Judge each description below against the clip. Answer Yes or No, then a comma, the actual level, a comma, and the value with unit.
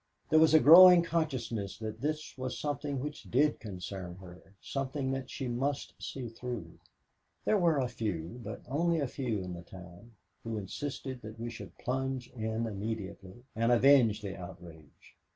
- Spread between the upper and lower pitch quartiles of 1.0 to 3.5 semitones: No, average, 5.2 semitones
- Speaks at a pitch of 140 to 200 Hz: No, low, 120 Hz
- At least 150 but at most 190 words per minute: Yes, average, 165 wpm